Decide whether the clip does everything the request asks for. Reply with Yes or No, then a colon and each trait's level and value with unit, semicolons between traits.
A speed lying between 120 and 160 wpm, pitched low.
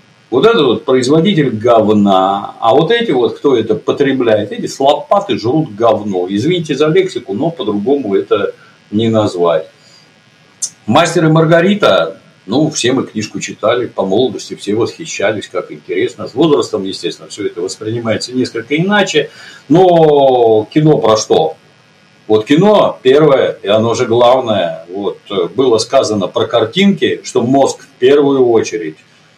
No: average, 135 wpm; medium, 160 Hz